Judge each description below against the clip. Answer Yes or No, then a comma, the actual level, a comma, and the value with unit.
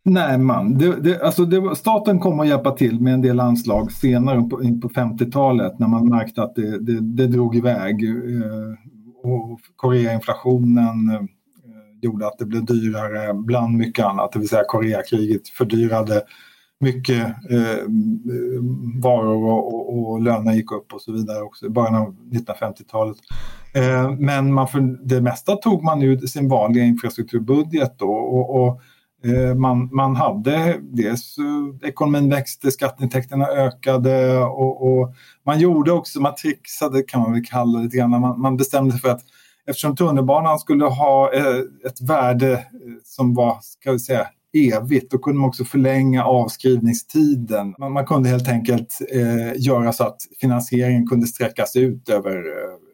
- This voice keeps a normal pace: Yes, average, 155 wpm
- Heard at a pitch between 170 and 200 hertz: No, low, 125 Hz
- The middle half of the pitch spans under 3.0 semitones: Yes, narrow, 2.6 semitones